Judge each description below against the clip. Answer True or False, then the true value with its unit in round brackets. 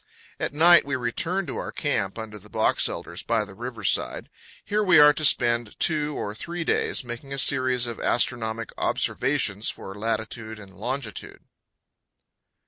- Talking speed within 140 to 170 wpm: True (160 wpm)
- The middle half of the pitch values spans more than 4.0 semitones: True (4.8 semitones)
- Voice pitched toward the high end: False (120 Hz)